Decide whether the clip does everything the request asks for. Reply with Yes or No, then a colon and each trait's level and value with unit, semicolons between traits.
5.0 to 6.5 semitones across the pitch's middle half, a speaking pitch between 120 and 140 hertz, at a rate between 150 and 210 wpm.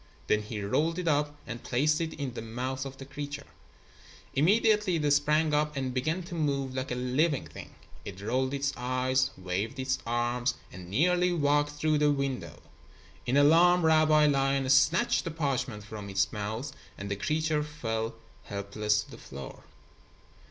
No: average, 4.3 semitones; low, 135 Hz; average, 165 wpm